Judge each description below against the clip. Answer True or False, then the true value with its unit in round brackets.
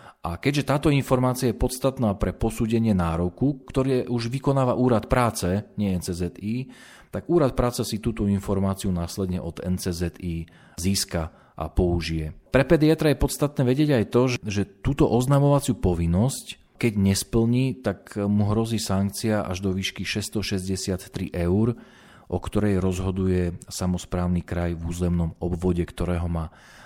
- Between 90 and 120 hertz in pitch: True (100 Hz)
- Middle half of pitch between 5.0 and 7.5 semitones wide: True (5.6 semitones)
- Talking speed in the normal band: True (135 wpm)